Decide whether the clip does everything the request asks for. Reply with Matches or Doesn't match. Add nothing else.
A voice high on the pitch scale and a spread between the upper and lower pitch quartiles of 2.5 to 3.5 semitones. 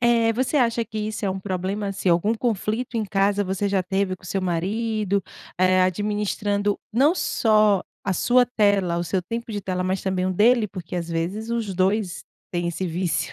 Matches